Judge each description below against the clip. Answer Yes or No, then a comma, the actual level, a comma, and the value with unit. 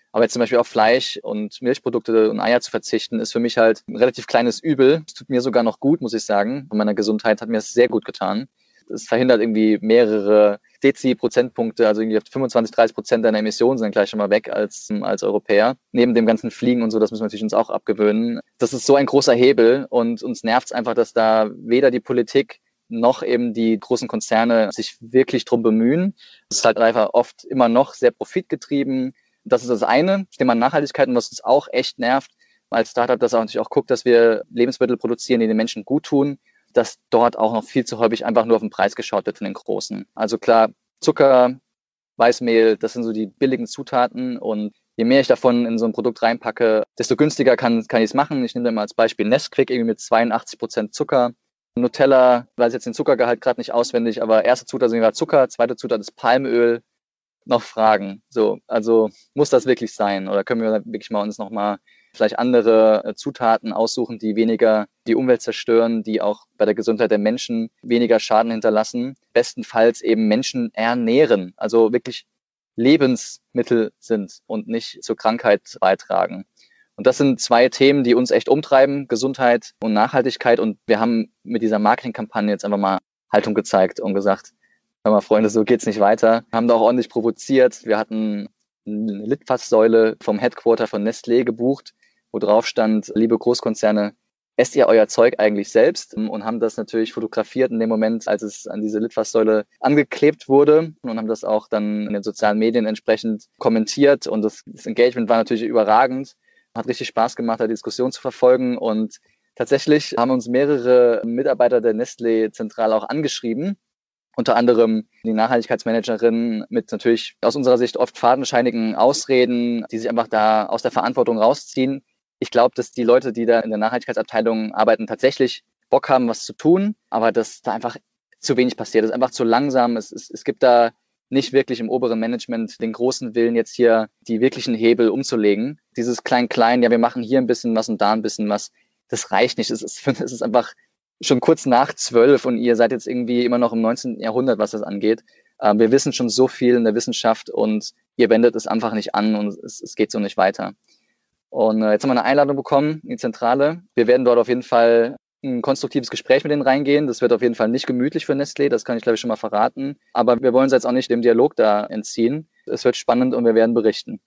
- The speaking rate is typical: No, fast, 200 wpm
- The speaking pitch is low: Yes, low, 115 Hz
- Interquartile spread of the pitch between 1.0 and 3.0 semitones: Yes, narrow, 2.4 semitones